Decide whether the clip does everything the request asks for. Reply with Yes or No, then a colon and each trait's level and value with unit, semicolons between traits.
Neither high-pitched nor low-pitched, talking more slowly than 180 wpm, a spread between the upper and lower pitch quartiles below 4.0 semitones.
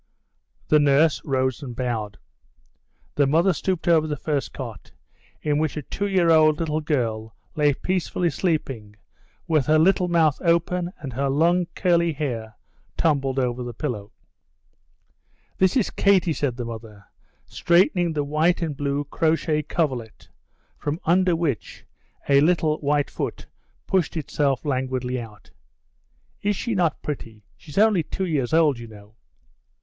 No: medium, 150 Hz; average, 145 wpm; average, 4.5 semitones